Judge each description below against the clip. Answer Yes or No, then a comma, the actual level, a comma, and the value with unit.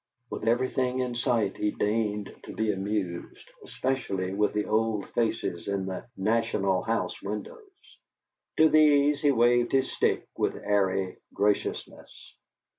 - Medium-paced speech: No, slow, 130 wpm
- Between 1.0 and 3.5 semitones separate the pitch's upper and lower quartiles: No, average, 4.0 semitones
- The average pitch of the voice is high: No, low, 110 Hz